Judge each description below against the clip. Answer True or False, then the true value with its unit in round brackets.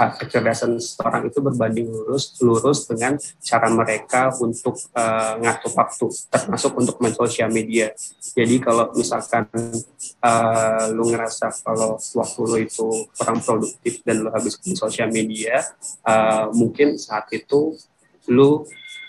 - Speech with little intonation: True (1.9 semitones)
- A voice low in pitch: True (115 Hz)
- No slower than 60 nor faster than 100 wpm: False (130 wpm)